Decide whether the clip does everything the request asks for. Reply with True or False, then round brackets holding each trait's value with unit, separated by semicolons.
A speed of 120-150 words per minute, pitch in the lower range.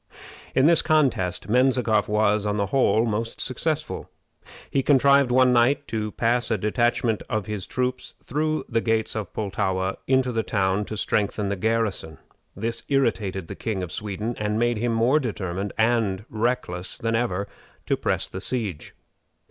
False (160 wpm; 110 Hz)